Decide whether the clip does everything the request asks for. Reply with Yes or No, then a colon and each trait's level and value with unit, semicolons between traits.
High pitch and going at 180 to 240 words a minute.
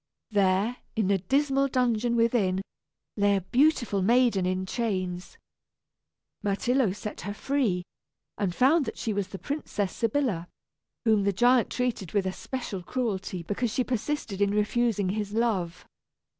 No: high, 210 Hz; average, 140 wpm